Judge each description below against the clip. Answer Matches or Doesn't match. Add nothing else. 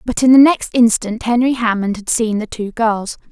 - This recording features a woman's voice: Matches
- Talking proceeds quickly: Matches